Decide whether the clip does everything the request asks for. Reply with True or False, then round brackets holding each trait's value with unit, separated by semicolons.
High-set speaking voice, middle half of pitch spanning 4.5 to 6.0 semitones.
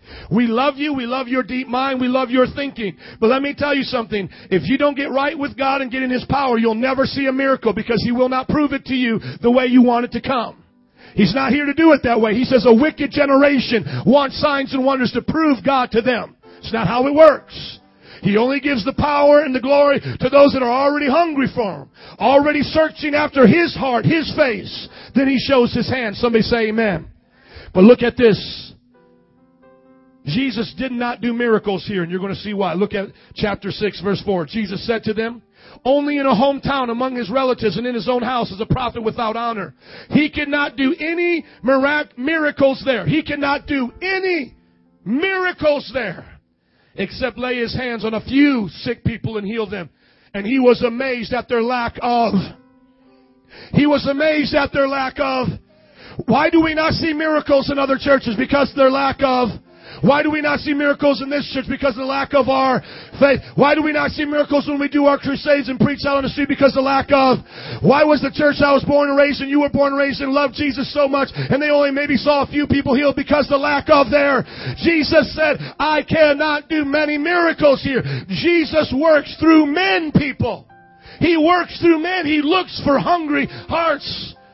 False (265 Hz; 3.7 semitones)